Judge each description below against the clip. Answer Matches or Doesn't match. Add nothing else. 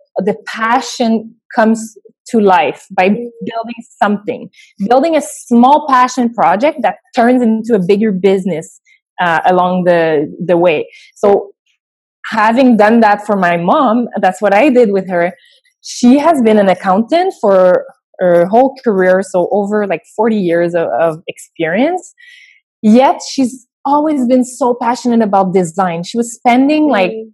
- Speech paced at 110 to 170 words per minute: Matches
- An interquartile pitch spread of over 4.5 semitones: Matches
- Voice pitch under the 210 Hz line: Doesn't match